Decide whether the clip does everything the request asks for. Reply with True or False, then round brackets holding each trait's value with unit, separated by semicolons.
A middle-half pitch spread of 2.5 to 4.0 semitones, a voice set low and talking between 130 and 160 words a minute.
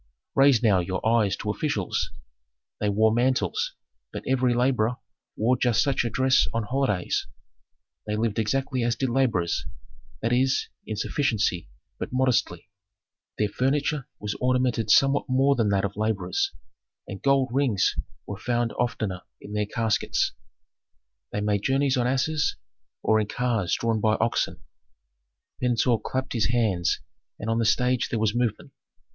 True (3.5 semitones; 115 Hz; 150 wpm)